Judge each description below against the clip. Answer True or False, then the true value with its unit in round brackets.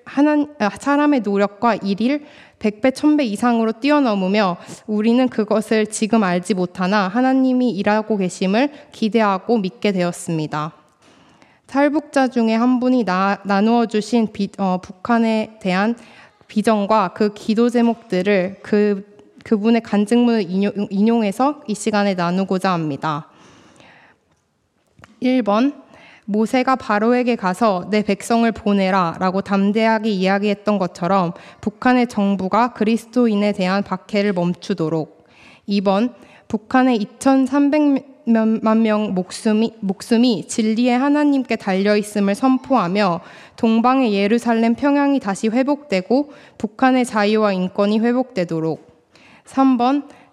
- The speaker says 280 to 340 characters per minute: False (260 characters per minute)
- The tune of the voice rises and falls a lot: False (3.5 semitones)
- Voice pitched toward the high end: True (220 Hz)